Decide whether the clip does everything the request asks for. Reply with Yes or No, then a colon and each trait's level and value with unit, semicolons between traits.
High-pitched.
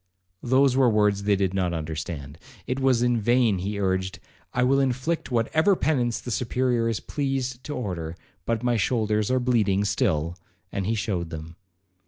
No: low, 115 Hz